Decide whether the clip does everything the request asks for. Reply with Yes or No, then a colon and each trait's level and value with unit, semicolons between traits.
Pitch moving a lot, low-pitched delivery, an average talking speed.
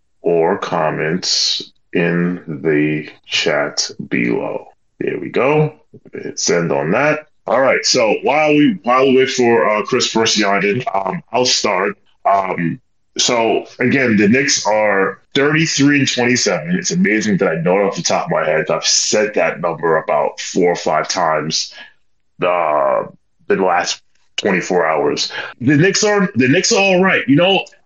Yes: wide, 6.8 semitones; low, 130 Hz; average, 165 wpm